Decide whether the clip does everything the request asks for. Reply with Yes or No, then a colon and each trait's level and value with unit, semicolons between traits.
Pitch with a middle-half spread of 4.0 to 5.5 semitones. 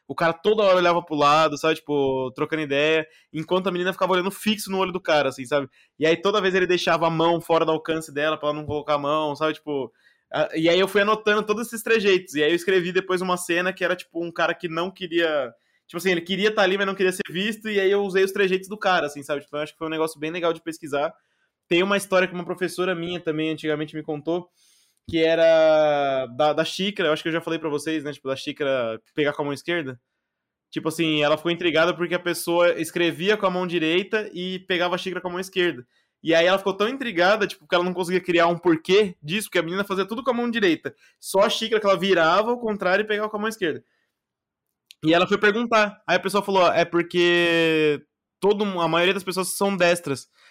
No: average, 3.3 semitones